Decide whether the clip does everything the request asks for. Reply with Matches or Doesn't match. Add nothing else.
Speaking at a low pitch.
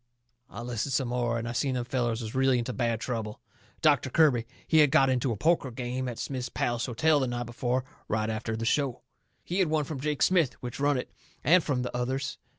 Matches